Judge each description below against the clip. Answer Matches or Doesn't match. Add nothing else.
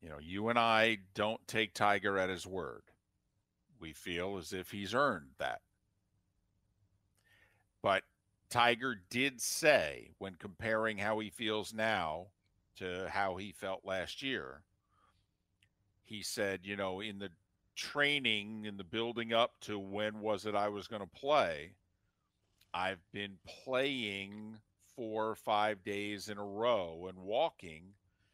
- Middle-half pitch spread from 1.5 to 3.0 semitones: Matches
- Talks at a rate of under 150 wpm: Matches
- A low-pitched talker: Matches